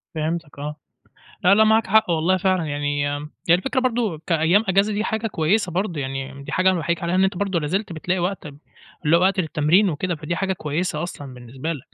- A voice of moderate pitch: Yes, medium, 170 Hz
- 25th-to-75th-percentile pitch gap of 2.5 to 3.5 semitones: No, average, 4.2 semitones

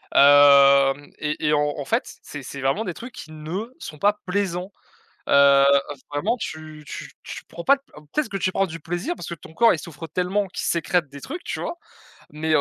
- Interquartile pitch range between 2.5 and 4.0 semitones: No, average, 5.1 semitones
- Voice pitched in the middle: Yes, medium, 160 Hz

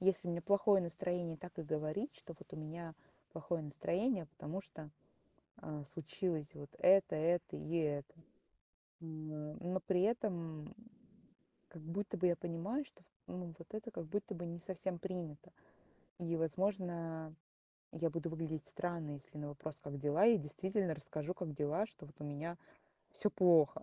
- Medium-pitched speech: Yes, medium, 170 Hz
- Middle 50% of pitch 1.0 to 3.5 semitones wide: Yes, average, 3.0 semitones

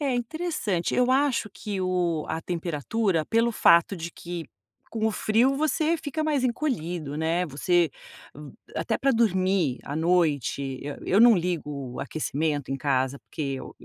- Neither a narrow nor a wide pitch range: No, wide, 7.0 semitones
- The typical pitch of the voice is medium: Yes, medium, 180 Hz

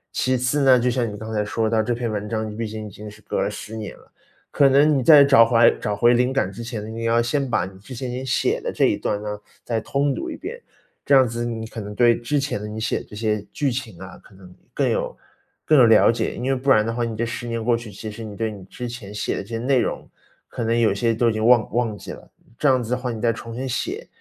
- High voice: No, low, 115 Hz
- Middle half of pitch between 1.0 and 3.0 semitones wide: Yes, average, 2.7 semitones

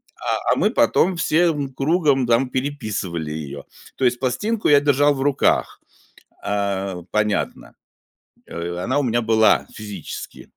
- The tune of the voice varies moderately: No, wide, 6.1 semitones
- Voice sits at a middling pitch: No, low, 125 Hz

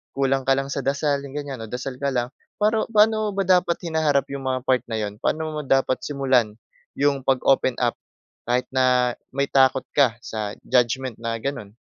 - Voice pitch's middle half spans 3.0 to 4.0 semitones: No, narrow, 2.5 semitones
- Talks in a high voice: No, low, 135 Hz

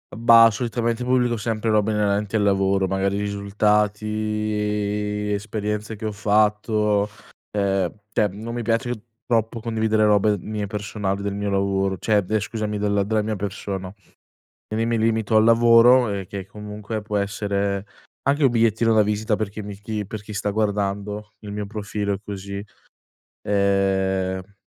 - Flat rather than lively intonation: Yes, narrow, 1.5 semitones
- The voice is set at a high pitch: No, low, 105 Hz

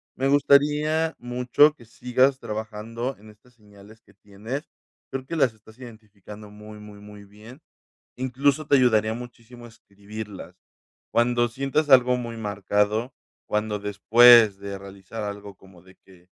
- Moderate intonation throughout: Yes, average, 3.4 semitones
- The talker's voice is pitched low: Yes, low, 110 Hz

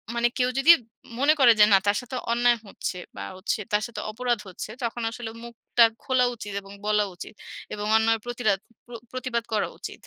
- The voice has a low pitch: No, high, 235 Hz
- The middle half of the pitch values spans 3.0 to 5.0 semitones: No, narrow, 2.6 semitones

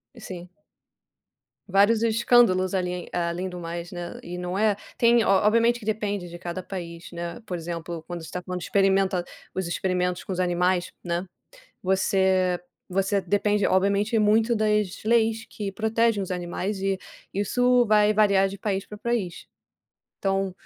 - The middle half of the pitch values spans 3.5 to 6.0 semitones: No, average, 2.9 semitones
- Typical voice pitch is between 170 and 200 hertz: Yes, high, 195 Hz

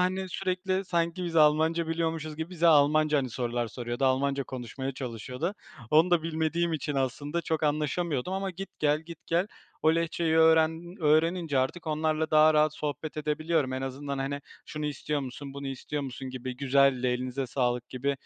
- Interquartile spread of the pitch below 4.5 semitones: Yes, average, 3.4 semitones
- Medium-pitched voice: Yes, medium, 150 Hz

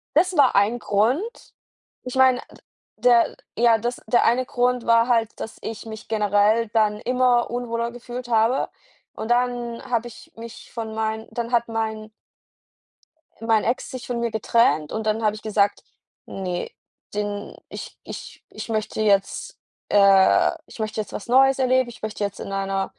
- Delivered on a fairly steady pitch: Yes, narrow, 2.2 semitones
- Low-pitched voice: No, high, 230 Hz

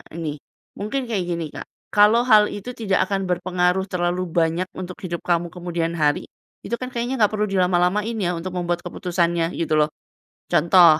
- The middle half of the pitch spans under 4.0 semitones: Yes, average, 2.9 semitones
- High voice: No, medium, 180 Hz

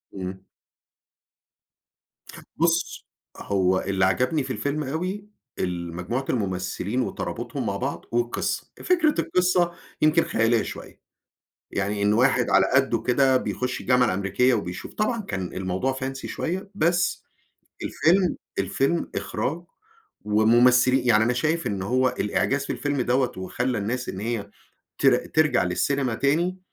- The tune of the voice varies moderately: No, wide, 6.9 semitones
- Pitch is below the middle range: Yes, low, 125 Hz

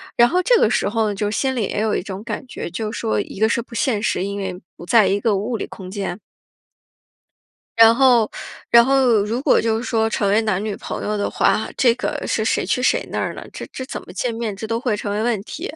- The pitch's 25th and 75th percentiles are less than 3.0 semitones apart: Yes, narrow, 2.6 semitones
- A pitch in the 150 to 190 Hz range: No, high, 220 Hz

